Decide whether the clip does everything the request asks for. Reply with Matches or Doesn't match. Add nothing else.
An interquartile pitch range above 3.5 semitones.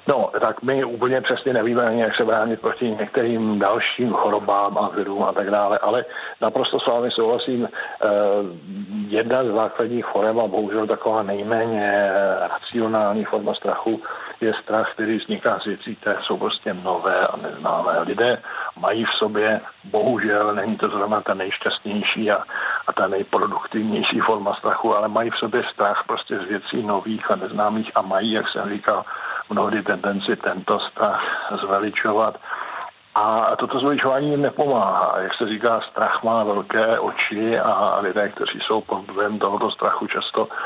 Doesn't match